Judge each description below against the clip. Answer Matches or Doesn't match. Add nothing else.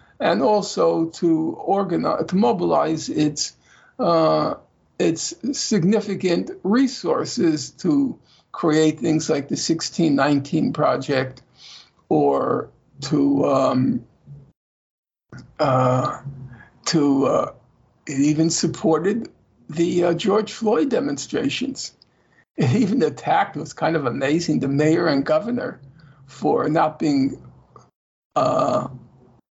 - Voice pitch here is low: Doesn't match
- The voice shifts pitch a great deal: Matches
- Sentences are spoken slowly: Matches